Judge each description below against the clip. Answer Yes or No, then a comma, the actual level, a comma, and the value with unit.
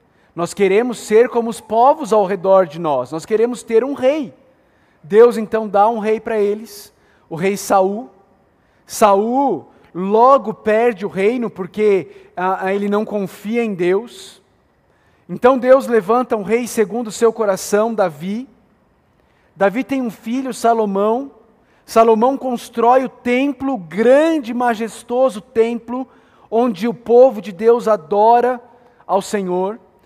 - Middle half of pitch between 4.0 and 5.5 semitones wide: No, average, 3.0 semitones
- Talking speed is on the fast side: No, average, 135 wpm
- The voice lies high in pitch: Yes, high, 225 Hz